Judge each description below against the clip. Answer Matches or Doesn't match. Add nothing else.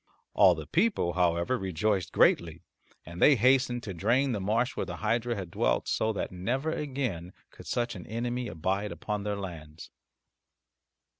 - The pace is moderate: Matches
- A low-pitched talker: Matches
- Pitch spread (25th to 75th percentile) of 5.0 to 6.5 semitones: Matches